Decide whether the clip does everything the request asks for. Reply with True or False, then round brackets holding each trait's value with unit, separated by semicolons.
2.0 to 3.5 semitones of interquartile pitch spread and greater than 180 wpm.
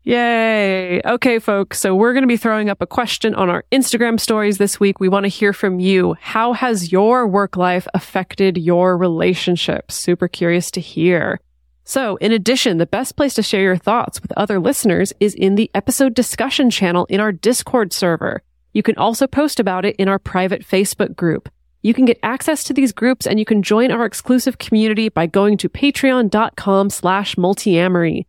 False (4.2 semitones; 190 wpm)